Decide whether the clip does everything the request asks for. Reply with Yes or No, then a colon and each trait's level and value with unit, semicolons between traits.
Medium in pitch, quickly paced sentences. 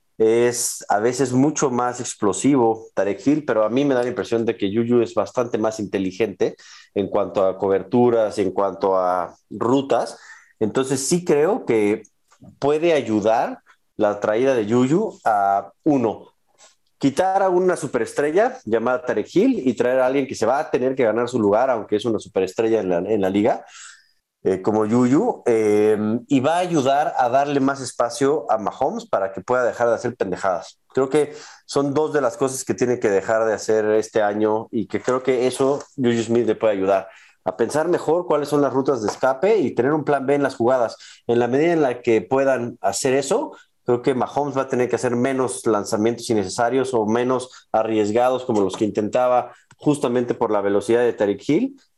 No: low, 120 Hz; fast, 195 wpm